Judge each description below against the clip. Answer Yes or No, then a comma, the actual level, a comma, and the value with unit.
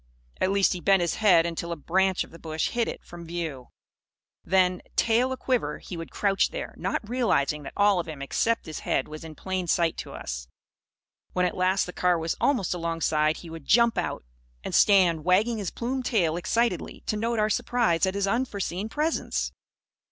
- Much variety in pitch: No, average, 4.7 semitones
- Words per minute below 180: No, average, 195 wpm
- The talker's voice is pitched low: No, medium, 185 Hz